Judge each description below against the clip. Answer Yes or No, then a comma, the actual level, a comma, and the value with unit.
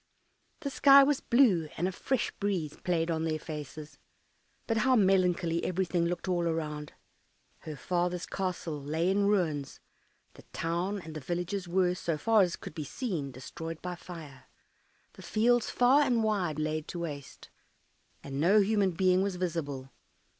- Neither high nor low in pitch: Yes, medium, 175 Hz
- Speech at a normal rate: Yes, average, 160 wpm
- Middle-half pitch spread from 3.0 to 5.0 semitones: Yes, average, 4.1 semitones